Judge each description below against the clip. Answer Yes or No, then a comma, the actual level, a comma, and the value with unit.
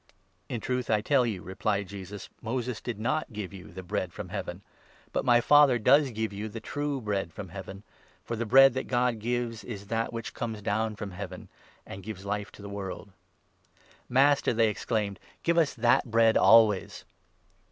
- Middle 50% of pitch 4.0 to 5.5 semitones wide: No, average, 3.4 semitones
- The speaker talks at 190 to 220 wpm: Yes, average, 200 wpm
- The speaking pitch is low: Yes, low, 110 Hz